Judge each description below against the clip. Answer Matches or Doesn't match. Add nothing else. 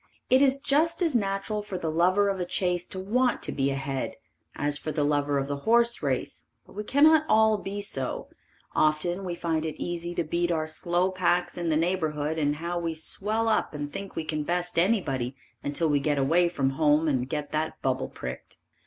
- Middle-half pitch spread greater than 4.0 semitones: Matches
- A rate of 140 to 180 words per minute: Doesn't match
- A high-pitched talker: Doesn't match